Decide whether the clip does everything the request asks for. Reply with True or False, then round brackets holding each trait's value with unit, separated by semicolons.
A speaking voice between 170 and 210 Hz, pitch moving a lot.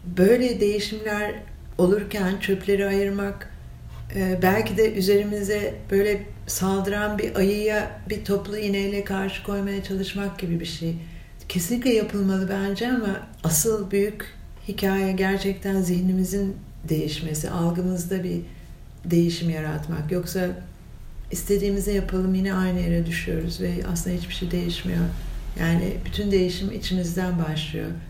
False (190 Hz; 2.5 semitones)